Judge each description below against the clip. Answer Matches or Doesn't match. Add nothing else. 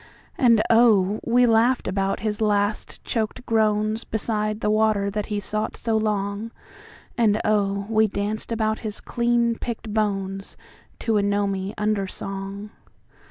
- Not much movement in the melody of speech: Matches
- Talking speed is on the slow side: Matches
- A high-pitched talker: Matches